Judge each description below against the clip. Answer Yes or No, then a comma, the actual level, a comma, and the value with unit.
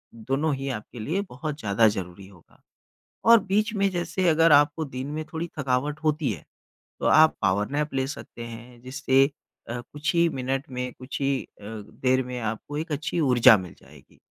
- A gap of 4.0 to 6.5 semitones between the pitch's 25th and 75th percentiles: Yes, average, 4.6 semitones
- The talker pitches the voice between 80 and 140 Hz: Yes, low, 135 Hz